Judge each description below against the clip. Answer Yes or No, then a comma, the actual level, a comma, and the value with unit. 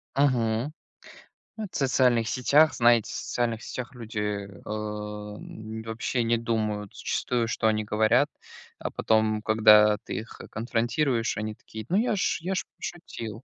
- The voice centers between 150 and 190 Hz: No, low, 115 Hz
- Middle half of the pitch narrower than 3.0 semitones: Yes, narrow, 2.6 semitones